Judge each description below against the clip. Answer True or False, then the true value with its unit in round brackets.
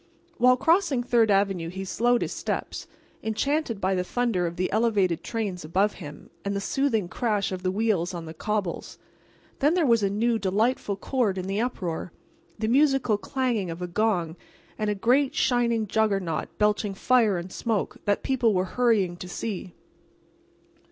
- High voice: True (210 Hz)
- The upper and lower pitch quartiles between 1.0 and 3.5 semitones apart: False (4.3 semitones)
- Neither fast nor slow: True (170 wpm)